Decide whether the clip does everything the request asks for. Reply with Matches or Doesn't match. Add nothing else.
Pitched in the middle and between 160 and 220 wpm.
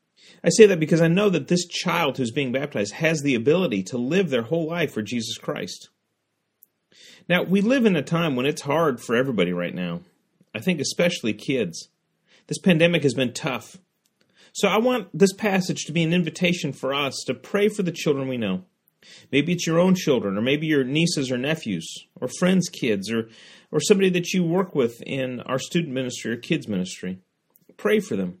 Matches